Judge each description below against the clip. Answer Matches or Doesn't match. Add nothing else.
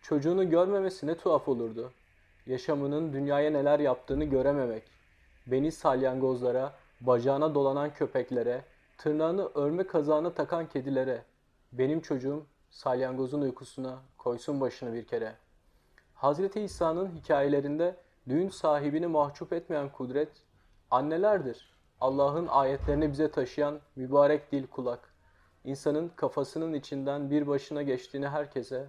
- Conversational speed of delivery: Matches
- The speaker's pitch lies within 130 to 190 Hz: Matches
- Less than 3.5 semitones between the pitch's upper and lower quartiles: Matches